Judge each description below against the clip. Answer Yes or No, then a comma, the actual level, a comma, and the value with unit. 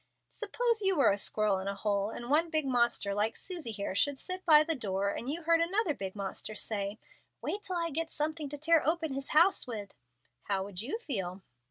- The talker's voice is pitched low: No, very high, 275 Hz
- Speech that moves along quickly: Yes, fast, 215 wpm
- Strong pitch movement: Yes, wide, 8.5 semitones